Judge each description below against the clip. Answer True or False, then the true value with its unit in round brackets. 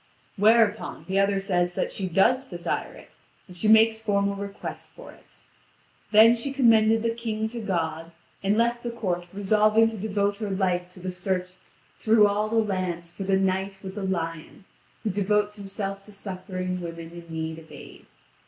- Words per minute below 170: False (180 wpm)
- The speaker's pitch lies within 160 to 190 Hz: False (200 Hz)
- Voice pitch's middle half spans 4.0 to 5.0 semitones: False (3.0 semitones)